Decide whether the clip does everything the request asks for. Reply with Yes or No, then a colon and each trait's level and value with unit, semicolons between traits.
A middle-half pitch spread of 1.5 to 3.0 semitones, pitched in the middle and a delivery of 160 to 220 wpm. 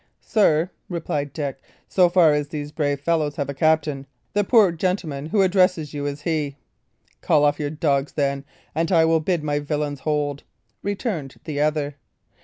Yes: average, 2.7 semitones; medium, 150 Hz; average, 175 wpm